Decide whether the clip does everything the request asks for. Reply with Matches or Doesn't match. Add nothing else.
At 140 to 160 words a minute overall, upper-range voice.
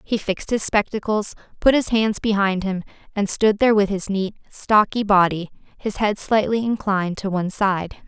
Doesn't match